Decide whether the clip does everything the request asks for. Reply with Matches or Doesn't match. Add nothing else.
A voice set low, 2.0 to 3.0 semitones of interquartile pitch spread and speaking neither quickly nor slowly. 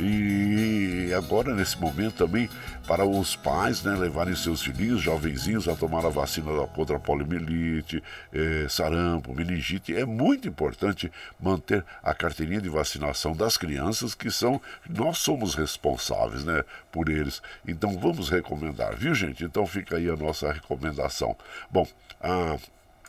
Doesn't match